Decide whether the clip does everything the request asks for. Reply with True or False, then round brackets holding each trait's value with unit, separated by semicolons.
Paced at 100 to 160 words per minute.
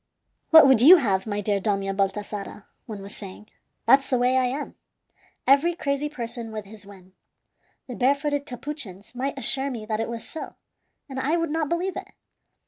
False (180 wpm)